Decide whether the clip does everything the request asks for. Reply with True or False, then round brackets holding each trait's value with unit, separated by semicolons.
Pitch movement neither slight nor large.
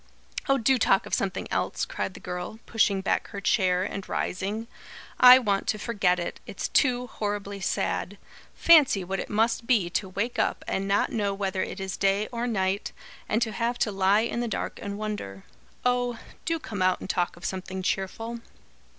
True (3.5 semitones)